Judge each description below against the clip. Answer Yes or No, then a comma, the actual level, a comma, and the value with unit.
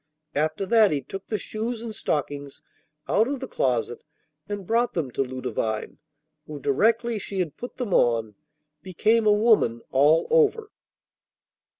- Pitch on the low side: No, high, 195 Hz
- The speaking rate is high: No, average, 150 wpm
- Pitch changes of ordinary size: No, wide, 8.5 semitones